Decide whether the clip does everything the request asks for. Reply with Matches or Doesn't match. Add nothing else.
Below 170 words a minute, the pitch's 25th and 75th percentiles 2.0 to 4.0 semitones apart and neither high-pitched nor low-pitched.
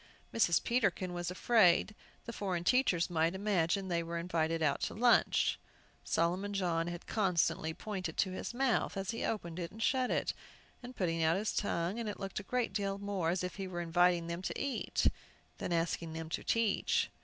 Doesn't match